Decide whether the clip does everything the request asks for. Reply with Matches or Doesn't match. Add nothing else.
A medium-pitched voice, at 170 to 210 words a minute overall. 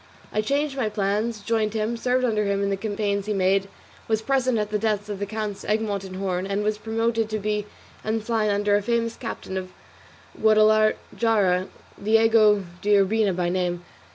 Doesn't match